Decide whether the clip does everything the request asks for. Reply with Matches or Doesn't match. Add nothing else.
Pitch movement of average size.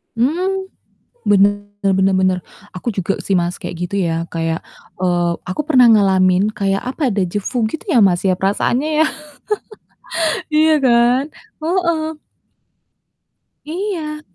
Doesn't match